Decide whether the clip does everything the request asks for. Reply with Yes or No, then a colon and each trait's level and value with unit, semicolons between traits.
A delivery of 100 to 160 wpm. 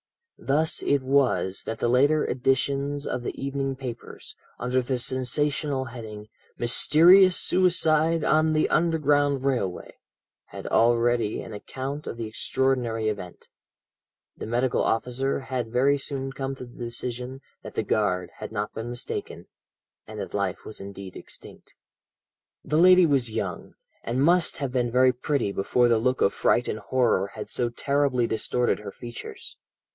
Yes: average, 150 wpm